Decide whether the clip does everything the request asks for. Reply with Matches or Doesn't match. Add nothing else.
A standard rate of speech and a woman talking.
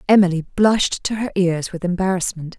Matches